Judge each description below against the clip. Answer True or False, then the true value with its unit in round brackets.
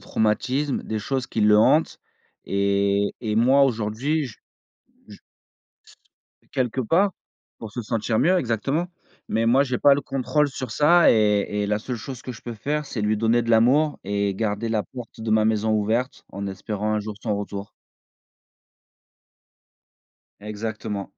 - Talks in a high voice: False (110 Hz)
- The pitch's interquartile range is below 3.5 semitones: False (3.8 semitones)